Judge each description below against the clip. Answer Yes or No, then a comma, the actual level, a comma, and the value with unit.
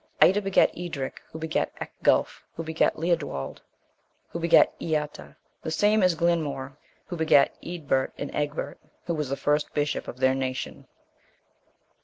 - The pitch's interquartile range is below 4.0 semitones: Yes, average, 3.3 semitones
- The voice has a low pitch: No, medium, 155 Hz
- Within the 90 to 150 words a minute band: Yes, average, 145 wpm